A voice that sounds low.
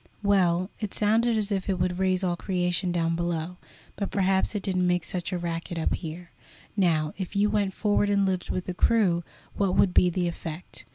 No: medium, 185 Hz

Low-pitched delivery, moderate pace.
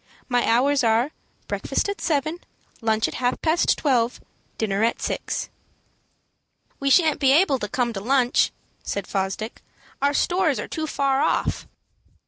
No: very high, 265 Hz; average, 150 wpm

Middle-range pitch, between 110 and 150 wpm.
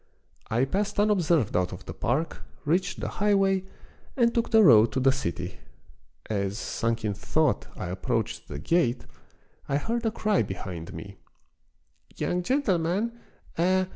Yes: medium, 160 Hz; average, 145 wpm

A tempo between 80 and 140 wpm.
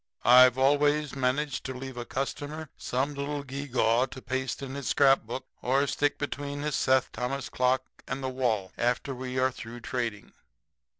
No: average, 165 wpm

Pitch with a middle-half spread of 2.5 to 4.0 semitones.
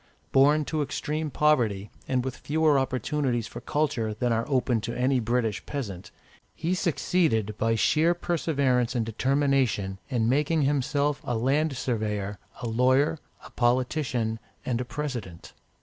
No: average, 4.5 semitones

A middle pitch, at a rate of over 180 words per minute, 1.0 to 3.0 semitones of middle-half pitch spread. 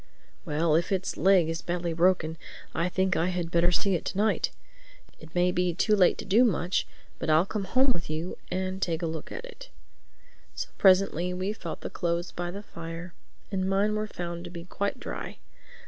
Yes: medium, 180 Hz; average, 200 wpm; narrow, 2.4 semitones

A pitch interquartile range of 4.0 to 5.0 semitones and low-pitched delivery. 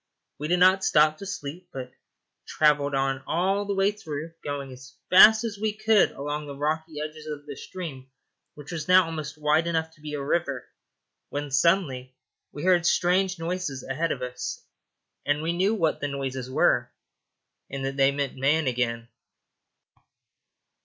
No: average, 4.3 semitones; medium, 150 Hz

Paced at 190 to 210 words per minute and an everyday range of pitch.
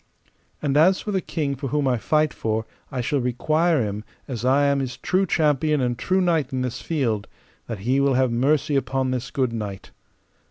Yes: average, 200 wpm; average, 3.8 semitones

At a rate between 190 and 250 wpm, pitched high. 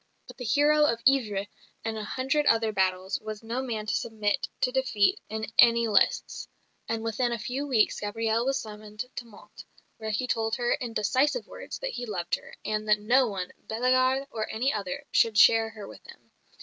Yes: average, 195 wpm; high, 225 Hz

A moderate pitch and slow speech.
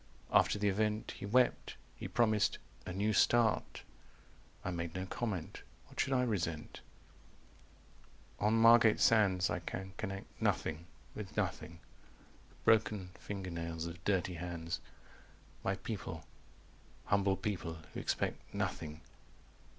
No: very low, 95 Hz; slow, 125 wpm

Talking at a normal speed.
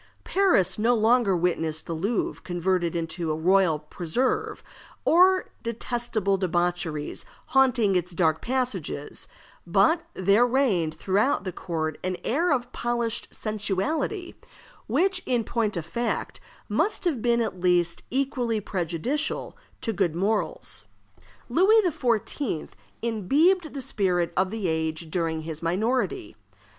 No: slow, 125 wpm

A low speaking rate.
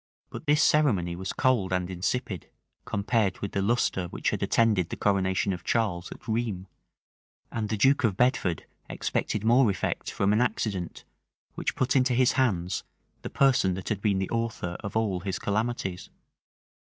No: average, 170 wpm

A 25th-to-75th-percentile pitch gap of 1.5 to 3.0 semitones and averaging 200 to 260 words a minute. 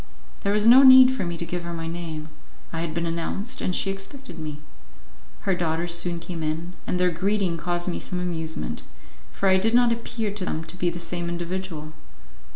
Yes: average, 2.7 semitones; fast, 205 wpm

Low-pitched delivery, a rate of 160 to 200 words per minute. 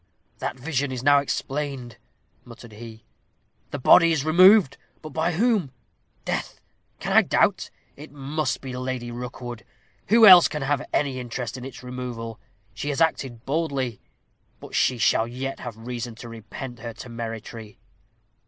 No: low, 130 Hz; average, 150 wpm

